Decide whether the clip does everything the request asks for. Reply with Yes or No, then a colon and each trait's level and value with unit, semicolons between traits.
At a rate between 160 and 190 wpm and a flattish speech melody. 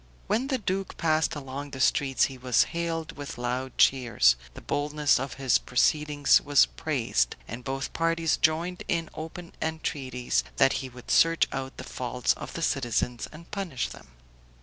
No: average, 165 wpm; average, 4.1 semitones